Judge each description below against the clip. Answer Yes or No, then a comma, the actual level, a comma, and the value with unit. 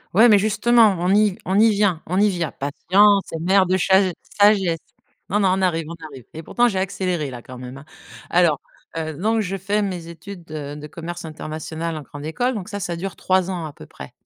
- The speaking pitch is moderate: Yes, medium, 180 Hz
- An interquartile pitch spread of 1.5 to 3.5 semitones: No, average, 4.0 semitones